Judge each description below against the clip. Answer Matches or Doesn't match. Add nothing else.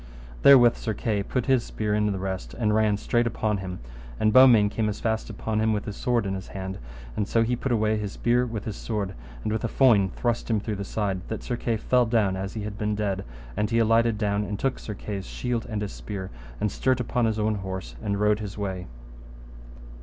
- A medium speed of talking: Doesn't match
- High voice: Doesn't match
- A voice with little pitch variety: Matches